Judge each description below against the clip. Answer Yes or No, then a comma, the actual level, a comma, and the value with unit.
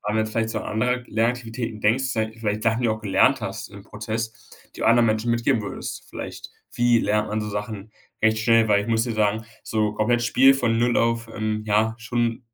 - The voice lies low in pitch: Yes, low, 110 Hz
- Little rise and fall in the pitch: Yes, narrow, 1.6 semitones